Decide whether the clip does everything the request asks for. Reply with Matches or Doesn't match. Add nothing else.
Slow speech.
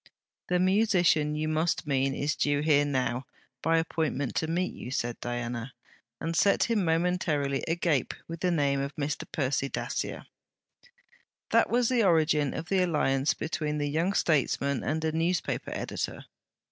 Doesn't match